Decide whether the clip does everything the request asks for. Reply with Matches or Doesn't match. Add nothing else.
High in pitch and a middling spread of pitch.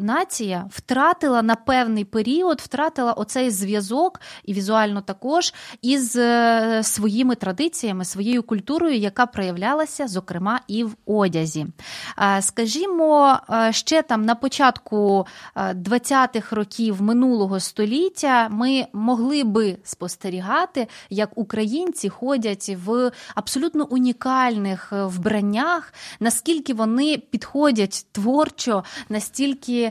Matches